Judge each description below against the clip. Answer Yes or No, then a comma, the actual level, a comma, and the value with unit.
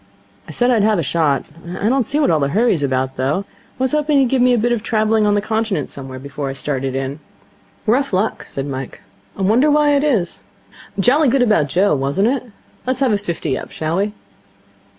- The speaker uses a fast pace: Yes, fast, 215 wpm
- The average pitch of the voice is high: Yes, high, 205 Hz